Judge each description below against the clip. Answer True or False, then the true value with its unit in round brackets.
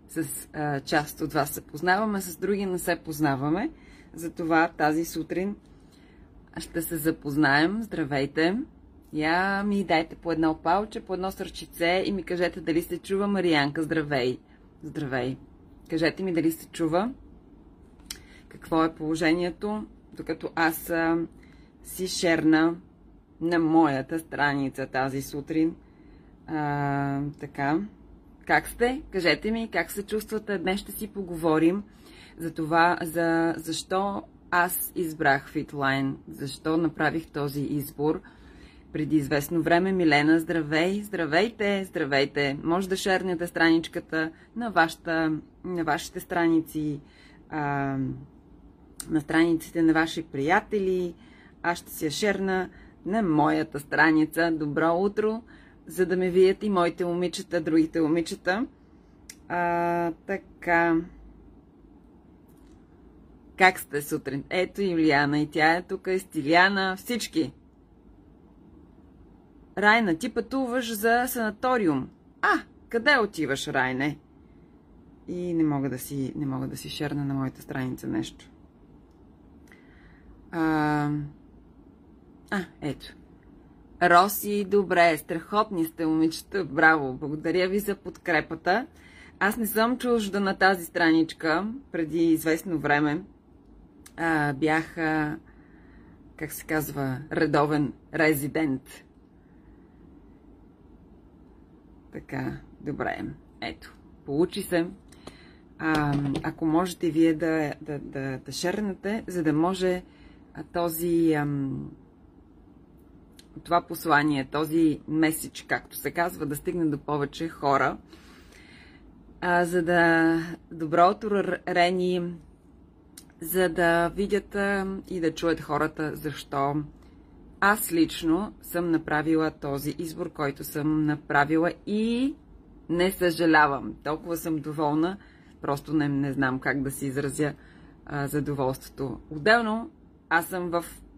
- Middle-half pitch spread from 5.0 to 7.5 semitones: False (3.2 semitones)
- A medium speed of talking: False (110 wpm)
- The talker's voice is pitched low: False (165 Hz)